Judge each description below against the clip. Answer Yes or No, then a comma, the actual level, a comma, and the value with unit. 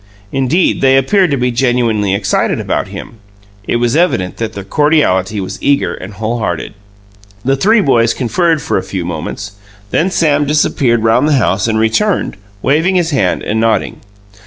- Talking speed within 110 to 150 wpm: No, average, 165 wpm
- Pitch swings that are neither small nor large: No, wide, 6.0 semitones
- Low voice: Yes, low, 120 Hz